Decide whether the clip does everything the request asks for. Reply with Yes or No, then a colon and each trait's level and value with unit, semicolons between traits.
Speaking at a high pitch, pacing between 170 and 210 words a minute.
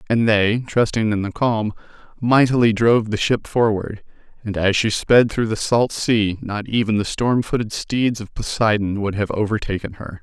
No: low, 110 Hz; average, 180 wpm